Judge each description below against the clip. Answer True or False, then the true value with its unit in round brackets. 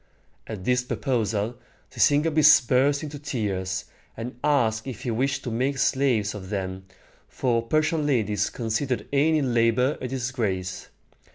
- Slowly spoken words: True (130 wpm)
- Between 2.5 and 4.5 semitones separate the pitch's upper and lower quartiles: True (4.2 semitones)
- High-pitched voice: False (125 Hz)